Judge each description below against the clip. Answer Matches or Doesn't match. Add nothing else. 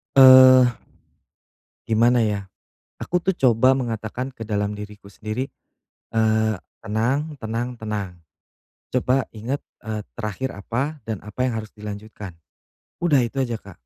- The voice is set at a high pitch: Doesn't match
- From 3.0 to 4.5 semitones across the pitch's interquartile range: Matches